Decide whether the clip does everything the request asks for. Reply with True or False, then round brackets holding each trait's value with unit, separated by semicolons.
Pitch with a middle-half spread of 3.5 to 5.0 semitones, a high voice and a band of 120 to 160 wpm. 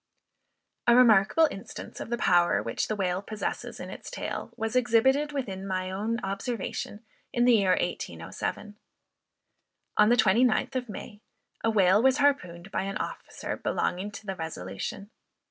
True (4.1 semitones; 210 Hz; 150 wpm)